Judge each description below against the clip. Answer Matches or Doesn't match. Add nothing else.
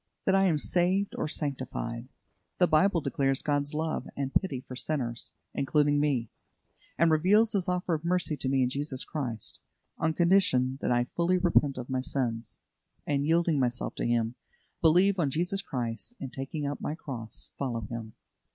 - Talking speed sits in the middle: Matches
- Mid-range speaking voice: Matches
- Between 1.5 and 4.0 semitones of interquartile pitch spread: Doesn't match